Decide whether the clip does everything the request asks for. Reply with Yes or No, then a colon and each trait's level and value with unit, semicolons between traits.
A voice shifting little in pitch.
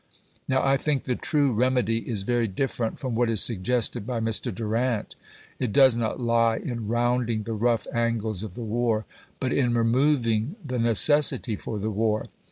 Yes: narrow, 2.2 semitones